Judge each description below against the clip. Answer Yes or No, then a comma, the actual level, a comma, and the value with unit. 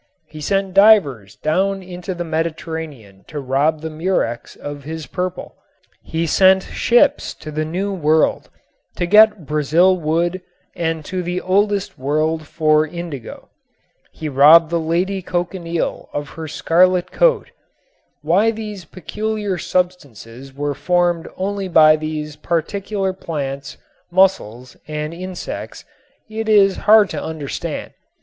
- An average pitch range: Yes, average, 3.6 semitones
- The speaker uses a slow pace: Yes, slow, 130 wpm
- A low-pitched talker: No, medium, 170 Hz